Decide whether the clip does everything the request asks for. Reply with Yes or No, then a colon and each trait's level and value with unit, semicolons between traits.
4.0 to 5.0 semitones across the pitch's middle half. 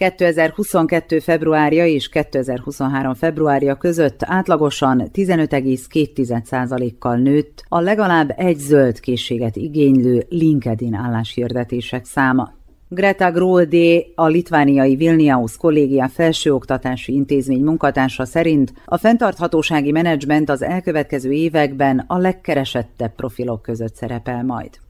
Yes: average, 4.3 semitones